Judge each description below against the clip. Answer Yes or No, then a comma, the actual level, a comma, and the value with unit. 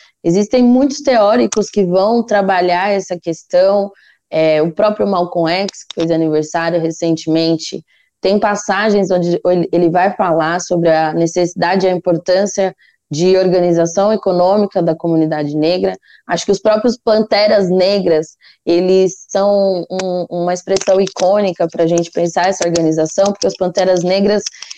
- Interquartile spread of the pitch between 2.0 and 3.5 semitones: Yes, average, 2.8 semitones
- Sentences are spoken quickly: No, average, 140 wpm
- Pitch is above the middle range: No, medium, 180 Hz